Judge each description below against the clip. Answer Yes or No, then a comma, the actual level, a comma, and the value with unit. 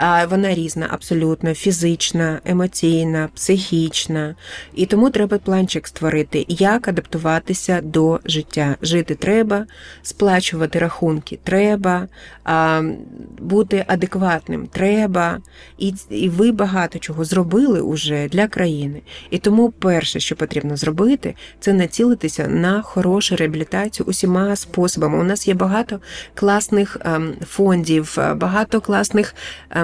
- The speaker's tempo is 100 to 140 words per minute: Yes, slow, 105 wpm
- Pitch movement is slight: No, average, 3.8 semitones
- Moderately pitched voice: Yes, medium, 180 Hz